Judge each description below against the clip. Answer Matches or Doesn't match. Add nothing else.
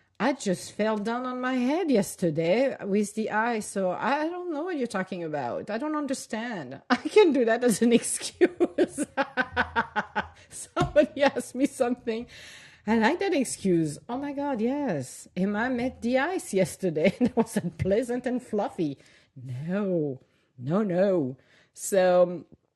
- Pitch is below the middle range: Doesn't match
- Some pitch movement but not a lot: Doesn't match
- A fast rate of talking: Doesn't match